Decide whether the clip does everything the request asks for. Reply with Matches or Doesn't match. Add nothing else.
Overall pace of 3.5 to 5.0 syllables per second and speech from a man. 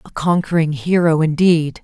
Doesn't match